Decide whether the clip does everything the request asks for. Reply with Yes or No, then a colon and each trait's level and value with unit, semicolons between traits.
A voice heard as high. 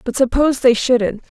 Yes: very high, 250 Hz